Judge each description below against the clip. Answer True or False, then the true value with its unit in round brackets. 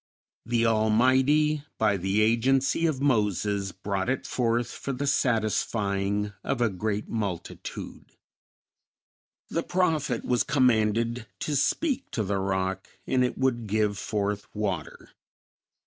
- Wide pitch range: False (4.2 semitones)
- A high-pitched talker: False (110 Hz)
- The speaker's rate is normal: False (120 wpm)